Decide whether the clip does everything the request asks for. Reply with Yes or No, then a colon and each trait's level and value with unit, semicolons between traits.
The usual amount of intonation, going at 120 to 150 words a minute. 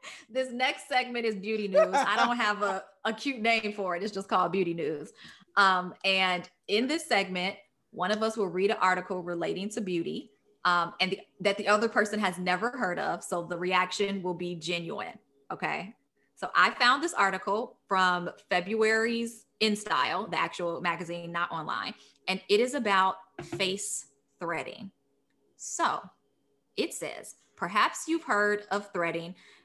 No: average, 3.4 semitones; average, 165 wpm